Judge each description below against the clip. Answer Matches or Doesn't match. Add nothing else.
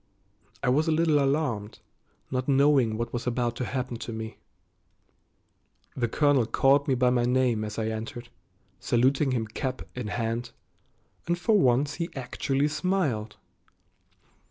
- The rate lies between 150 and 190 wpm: Doesn't match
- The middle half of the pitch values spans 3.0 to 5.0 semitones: Matches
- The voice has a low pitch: Matches